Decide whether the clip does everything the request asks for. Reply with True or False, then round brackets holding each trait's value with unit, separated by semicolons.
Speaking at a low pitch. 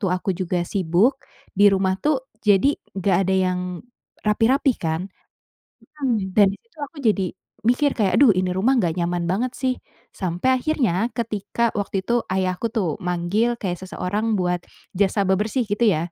False (200 Hz)